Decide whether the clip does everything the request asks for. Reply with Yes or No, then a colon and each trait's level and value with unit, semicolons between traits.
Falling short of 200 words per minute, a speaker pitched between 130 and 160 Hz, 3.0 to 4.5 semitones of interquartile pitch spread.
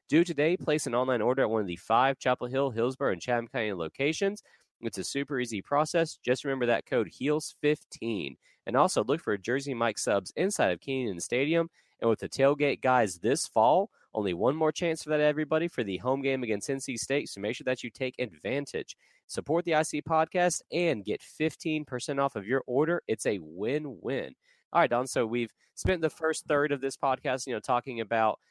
No: fast, 205 wpm; low, 135 Hz; average, 4.1 semitones